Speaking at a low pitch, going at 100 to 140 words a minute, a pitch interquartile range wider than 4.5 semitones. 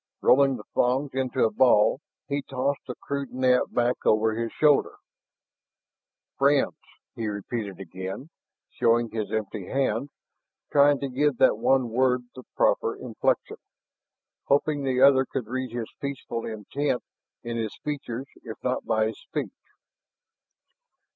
No: low, 125 Hz; slow, 135 wpm; average, 3.5 semitones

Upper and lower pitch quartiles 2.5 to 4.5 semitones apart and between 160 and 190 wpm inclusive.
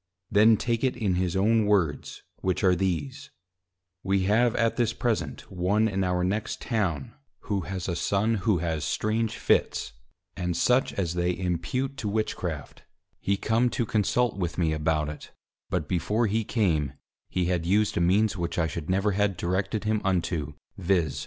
Yes: average, 4.0 semitones; average, 170 wpm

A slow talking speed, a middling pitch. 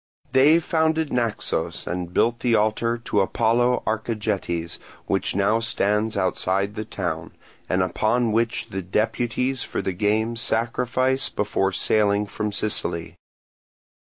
No: slow, 125 wpm; low, 110 Hz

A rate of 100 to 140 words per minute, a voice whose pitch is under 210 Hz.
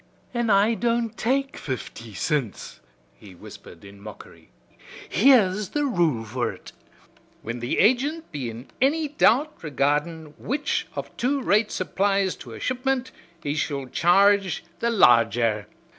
Yes: slow, 135 wpm; high, 190 Hz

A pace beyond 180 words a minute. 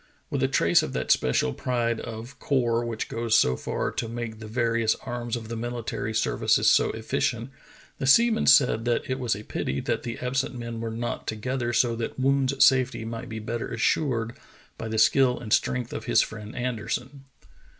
Yes: average, 190 wpm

